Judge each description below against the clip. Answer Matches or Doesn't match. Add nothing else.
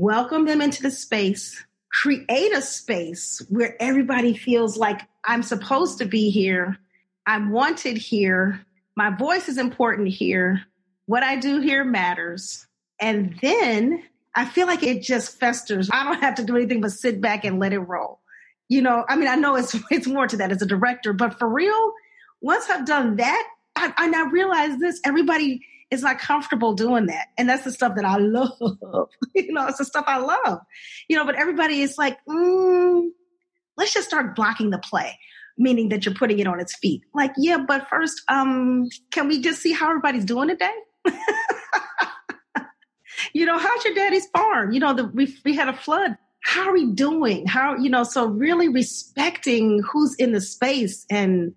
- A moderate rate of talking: Matches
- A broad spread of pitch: Matches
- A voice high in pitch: Matches